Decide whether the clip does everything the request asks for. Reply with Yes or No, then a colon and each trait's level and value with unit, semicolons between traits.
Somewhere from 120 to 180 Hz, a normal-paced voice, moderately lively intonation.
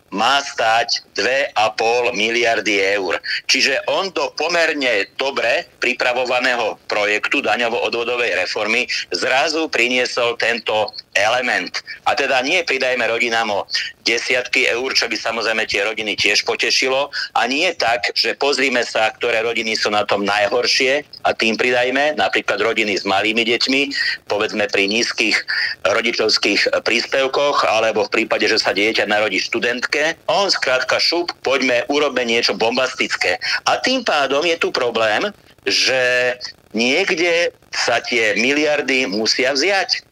Yes: low, 125 Hz; average, 130 wpm; average, 4.0 semitones